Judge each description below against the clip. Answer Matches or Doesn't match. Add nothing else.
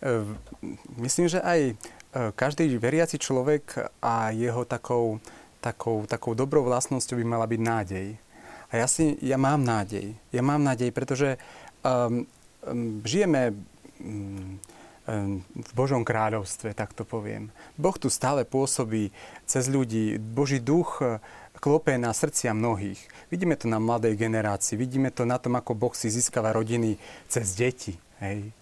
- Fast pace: Doesn't match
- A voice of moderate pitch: Doesn't match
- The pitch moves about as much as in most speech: Matches